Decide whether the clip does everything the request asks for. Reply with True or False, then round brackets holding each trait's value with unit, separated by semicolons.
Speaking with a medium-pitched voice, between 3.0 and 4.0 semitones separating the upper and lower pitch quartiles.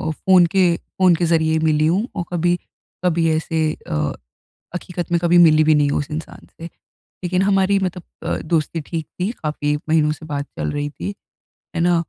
False (165 Hz; 2.5 semitones)